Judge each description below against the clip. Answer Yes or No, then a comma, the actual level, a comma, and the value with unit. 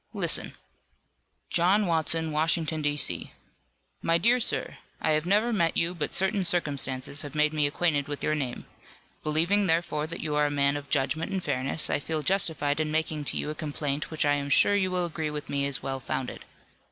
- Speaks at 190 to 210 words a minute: Yes, average, 200 wpm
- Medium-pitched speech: Yes, medium, 155 Hz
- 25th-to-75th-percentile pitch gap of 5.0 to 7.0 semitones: No, average, 2.7 semitones